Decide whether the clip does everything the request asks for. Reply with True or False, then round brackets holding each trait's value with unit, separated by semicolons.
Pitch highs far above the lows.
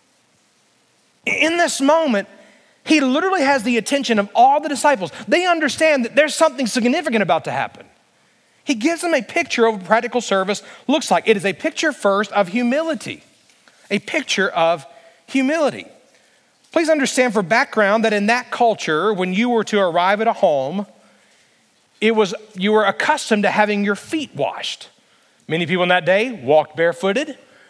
True (6.4 semitones)